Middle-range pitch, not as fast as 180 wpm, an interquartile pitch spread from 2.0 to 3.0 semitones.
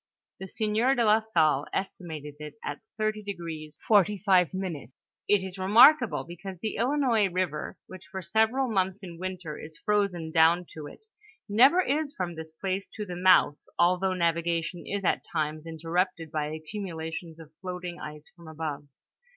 No: medium, 180 Hz; average, 150 wpm; average, 4.2 semitones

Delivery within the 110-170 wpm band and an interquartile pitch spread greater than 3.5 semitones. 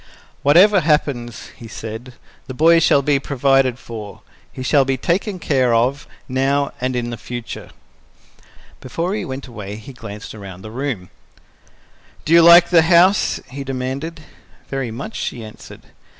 Yes: average, 150 wpm; average, 4.6 semitones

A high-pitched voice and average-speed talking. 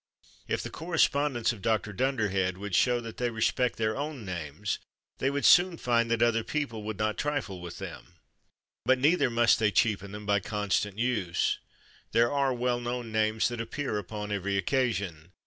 No: low, 115 Hz; average, 175 wpm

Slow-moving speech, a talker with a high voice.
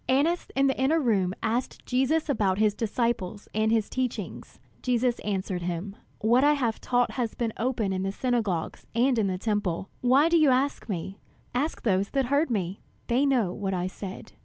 No: average, 185 wpm; high, 230 Hz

